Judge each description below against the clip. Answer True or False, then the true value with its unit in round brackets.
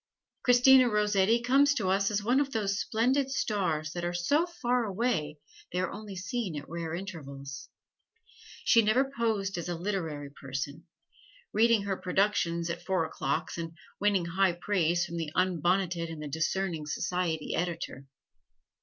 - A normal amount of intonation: True (4.7 semitones)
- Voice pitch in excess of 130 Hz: True (185 Hz)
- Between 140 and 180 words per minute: True (155 wpm)